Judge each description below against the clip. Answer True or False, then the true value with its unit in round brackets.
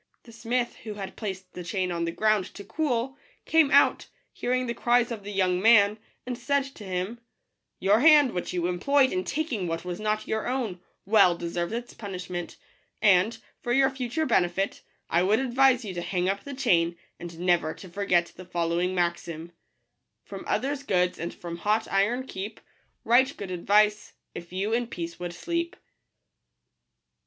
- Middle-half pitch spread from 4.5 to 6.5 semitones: True (5.3 semitones)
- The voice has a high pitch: True (205 Hz)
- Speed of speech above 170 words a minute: True (180 wpm)